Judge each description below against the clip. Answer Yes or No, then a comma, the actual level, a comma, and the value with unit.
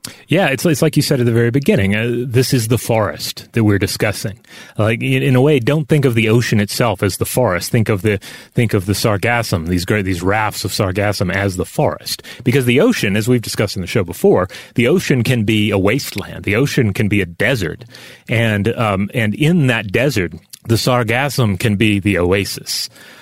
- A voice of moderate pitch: No, low, 115 Hz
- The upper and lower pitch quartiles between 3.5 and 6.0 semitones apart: Yes, average, 3.8 semitones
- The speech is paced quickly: Yes, fast, 215 wpm